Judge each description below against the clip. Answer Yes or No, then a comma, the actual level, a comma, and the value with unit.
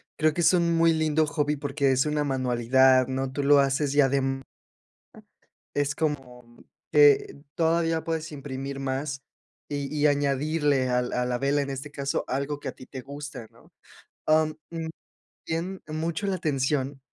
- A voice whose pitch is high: No, medium, 145 Hz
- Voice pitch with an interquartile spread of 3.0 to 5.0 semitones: No, narrow, 2.6 semitones